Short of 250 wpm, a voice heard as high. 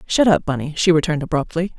No: average, 200 wpm; medium, 160 Hz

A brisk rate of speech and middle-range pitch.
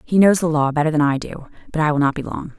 Yes: fast, 325 wpm; medium, 155 Hz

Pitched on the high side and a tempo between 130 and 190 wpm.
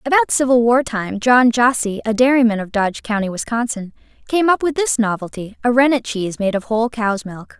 No: high, 235 Hz; average, 200 wpm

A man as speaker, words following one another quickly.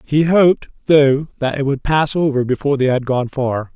Yes: male; fast, 210 wpm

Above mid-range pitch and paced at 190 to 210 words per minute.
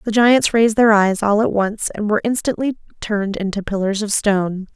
Yes: high, 210 Hz; average, 200 wpm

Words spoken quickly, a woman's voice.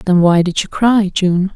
Yes: fast, 230 wpm; female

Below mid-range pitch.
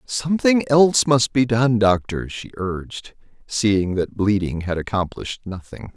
Yes: low, 110 Hz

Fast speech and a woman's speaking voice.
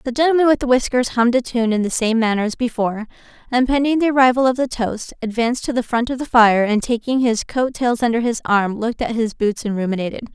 Yes: fast, 245 wpm; female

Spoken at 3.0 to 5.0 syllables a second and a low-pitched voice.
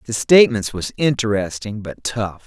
Yes: 4.8 syllables/s; low, 115 Hz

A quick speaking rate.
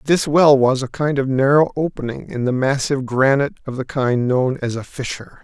Yes: fast, 210 wpm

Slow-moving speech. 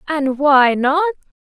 Yes: slow, 125 wpm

